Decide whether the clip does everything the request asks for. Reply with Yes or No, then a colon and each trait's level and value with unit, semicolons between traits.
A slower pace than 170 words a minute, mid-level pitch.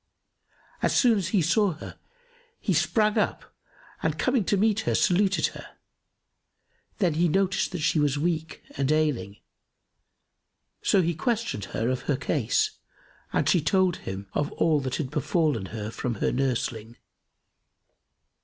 Yes: average, 145 wpm; medium, 160 Hz